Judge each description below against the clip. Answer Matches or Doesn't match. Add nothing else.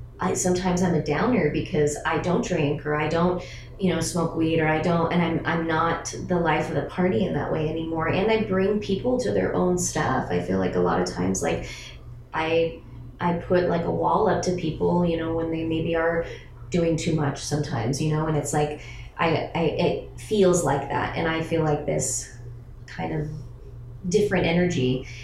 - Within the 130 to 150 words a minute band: Doesn't match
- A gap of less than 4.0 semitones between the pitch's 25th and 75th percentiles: Doesn't match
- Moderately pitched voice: Matches